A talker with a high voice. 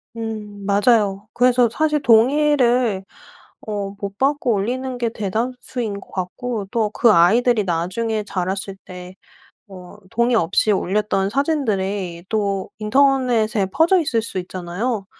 Yes: high, 215 Hz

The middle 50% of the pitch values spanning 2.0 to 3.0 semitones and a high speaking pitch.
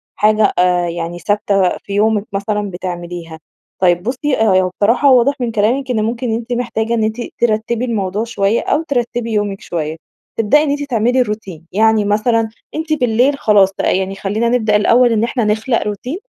No: average, 3.4 semitones; high, 220 Hz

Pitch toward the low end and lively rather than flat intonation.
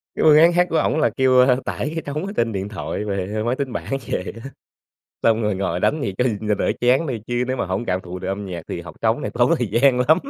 Yes: low, 120 Hz; wide, 5.8 semitones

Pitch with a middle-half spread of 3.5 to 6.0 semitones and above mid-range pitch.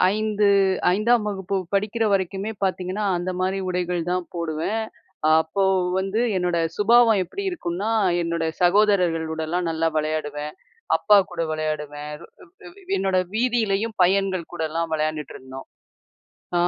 No: average, 4.4 semitones; medium, 180 Hz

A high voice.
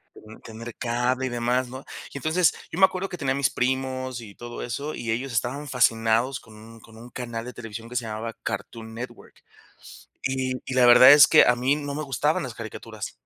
No: low, 125 Hz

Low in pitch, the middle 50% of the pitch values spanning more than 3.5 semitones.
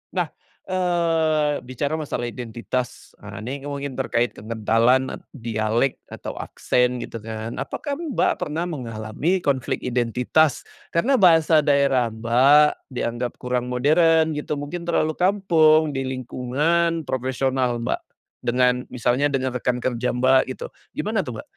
Yes: low, 130 Hz; average, 4.3 semitones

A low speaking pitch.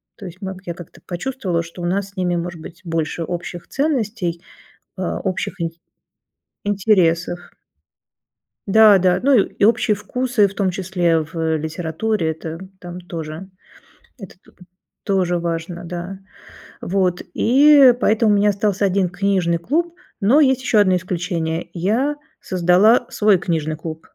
No: medium, 185 Hz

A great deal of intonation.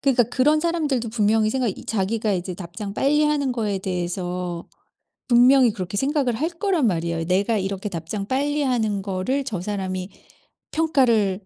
Yes: wide, 6.0 semitones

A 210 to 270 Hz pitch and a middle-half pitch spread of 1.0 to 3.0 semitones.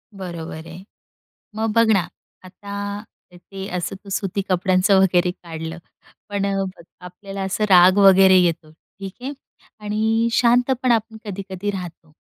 No: high, 195 Hz; narrow, 2.5 semitones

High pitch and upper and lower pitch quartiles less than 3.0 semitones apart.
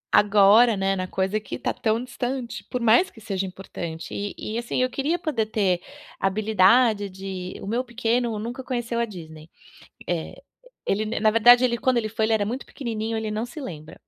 No: high, 220 Hz; average, 3.6 semitones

